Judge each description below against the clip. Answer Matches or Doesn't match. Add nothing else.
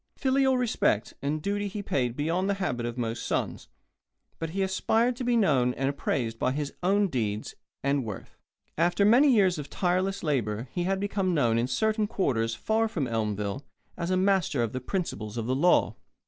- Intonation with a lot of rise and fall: Matches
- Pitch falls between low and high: Matches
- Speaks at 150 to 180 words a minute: Doesn't match